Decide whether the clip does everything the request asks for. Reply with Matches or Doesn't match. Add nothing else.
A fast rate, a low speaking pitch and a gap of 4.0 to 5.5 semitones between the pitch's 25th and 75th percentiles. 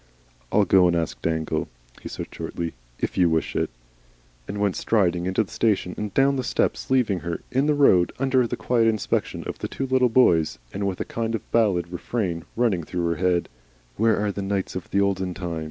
Matches